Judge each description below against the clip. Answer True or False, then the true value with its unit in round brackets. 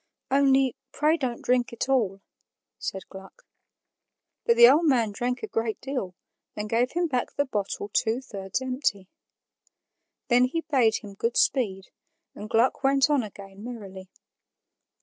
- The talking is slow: False (150 wpm)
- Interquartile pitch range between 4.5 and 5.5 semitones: True (4.8 semitones)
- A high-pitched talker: True (245 Hz)